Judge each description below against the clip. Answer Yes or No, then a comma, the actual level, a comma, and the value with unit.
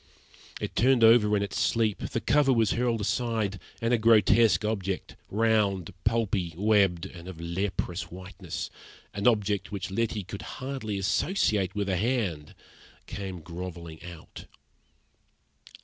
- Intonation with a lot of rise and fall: No, average, 3.7 semitones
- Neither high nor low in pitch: No, low, 100 Hz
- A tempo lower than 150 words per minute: Yes, slow, 135 wpm